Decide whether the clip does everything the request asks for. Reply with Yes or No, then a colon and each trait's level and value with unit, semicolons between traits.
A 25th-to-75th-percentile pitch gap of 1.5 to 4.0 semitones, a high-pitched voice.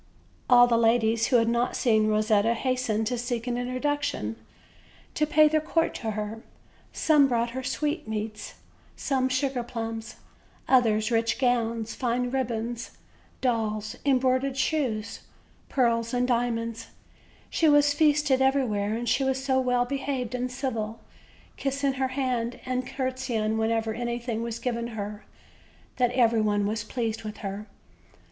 Yes: average, 2.7 semitones; high, 240 Hz